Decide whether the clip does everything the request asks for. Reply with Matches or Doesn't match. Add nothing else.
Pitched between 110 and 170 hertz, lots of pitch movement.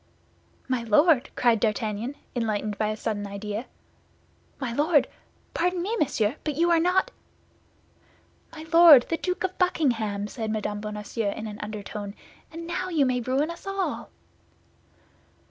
Doesn't match